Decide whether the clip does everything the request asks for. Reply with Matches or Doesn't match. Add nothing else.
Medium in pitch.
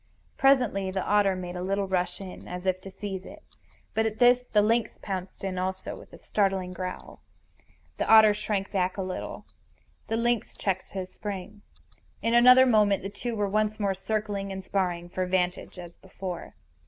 Doesn't match